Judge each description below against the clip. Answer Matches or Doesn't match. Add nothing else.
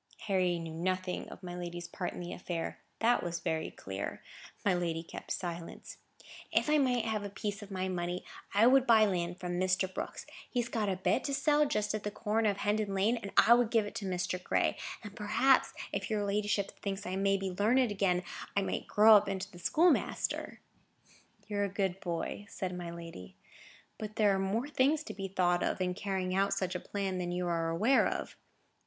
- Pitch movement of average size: Matches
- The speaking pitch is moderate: Doesn't match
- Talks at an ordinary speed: Doesn't match